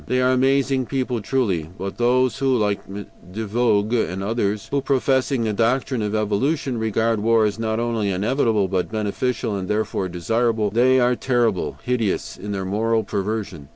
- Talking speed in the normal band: Yes, average, 165 wpm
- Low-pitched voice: Yes, low, 110 Hz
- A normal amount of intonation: Yes, average, 3.6 semitones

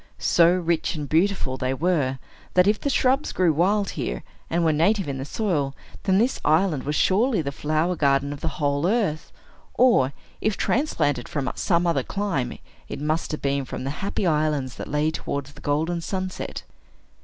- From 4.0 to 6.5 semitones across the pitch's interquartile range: Yes, average, 4.9 semitones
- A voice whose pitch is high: No, medium, 160 Hz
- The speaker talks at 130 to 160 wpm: No, average, 180 wpm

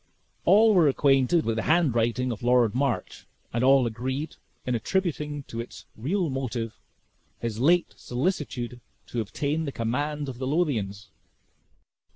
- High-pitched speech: No, low, 130 Hz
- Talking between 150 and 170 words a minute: No, average, 140 wpm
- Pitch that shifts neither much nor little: Yes, average, 4.3 semitones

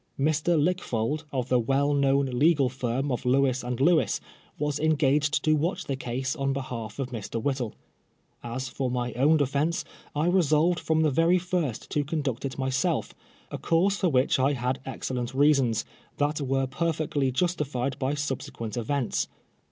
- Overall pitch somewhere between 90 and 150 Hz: Yes, medium, 140 Hz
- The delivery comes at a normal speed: Yes, average, 160 wpm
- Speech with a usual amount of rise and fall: Yes, average, 3.1 semitones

